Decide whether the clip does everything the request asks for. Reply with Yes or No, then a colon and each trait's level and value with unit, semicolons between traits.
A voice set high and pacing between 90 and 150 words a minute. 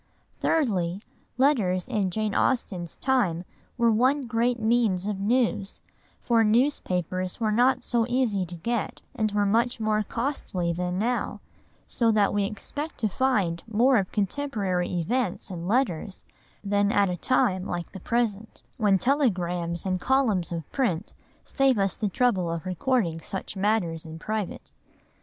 Yes: high, 210 Hz; average, 145 wpm